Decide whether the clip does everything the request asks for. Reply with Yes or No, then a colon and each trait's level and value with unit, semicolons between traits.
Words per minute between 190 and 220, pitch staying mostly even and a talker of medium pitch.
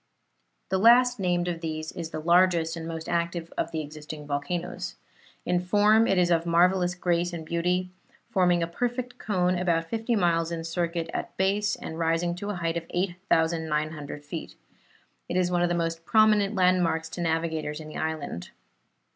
No: average, 175 wpm; narrow, 2.0 semitones; medium, 170 Hz